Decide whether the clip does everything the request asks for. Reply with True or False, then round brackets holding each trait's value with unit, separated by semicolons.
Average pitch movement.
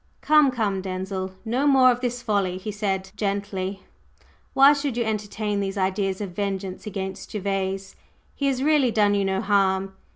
True (3.6 semitones)